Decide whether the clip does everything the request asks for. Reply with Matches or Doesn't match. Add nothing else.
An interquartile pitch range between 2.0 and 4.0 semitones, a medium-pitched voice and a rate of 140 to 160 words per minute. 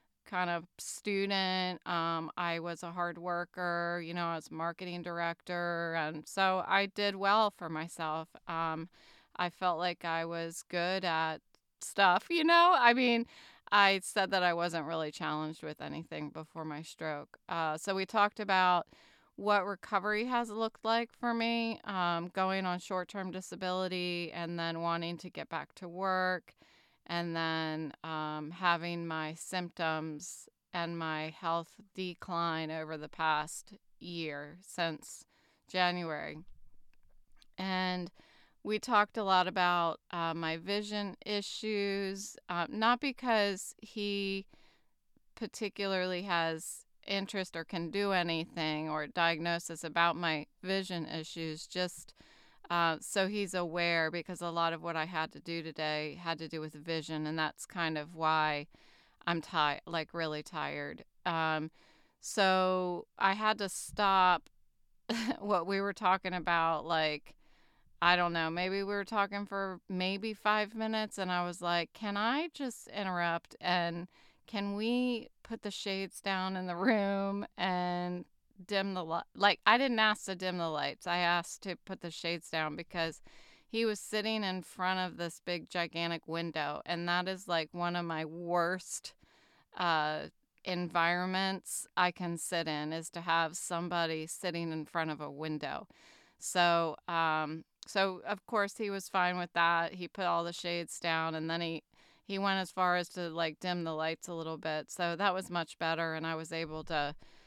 Matches